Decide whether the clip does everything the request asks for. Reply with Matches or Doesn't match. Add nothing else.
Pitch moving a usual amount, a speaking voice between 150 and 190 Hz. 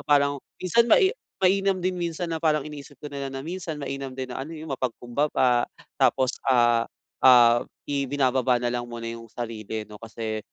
Doesn't match